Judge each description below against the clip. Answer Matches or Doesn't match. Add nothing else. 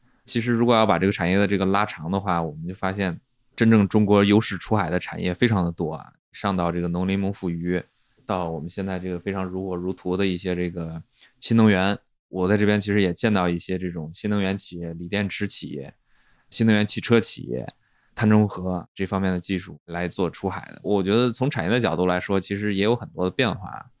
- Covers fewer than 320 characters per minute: Doesn't match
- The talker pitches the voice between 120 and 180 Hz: Doesn't match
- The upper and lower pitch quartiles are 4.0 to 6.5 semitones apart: Doesn't match